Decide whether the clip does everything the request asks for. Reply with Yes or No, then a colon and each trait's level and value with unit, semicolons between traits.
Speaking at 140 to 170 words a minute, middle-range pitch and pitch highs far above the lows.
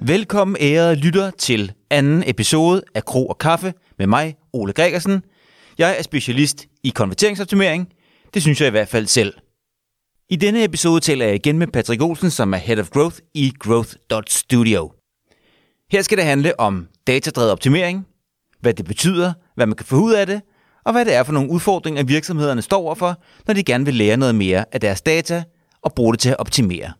No: average, 190 wpm; medium, 145 Hz; wide, 7.2 semitones